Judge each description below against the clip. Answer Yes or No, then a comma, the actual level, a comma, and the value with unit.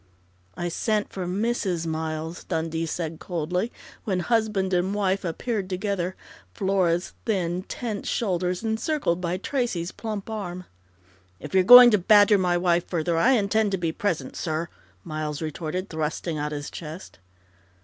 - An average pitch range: Yes, average, 3.7 semitones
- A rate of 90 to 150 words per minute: Yes, average, 145 wpm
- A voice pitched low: No, medium, 180 Hz